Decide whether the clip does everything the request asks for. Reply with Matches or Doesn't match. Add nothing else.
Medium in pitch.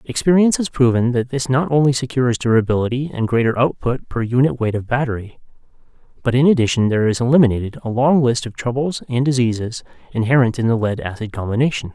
Doesn't match